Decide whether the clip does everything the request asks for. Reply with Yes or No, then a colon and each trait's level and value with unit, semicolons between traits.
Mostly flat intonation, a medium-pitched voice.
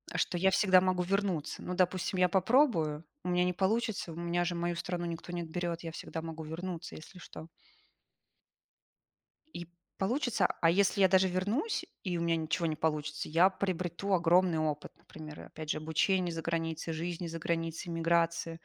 Yes: narrow, 2.2 semitones; medium, 170 Hz